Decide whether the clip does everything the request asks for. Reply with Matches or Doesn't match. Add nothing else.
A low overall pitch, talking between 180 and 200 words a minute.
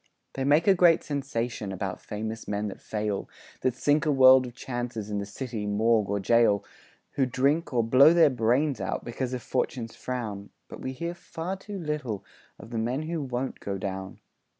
Matches